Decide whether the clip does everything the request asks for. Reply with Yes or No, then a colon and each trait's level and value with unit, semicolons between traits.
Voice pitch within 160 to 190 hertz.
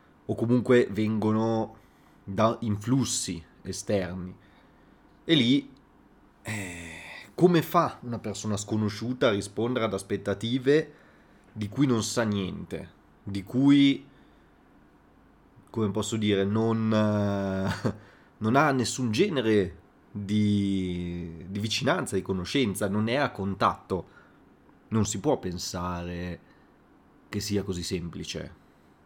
No: low, 105 Hz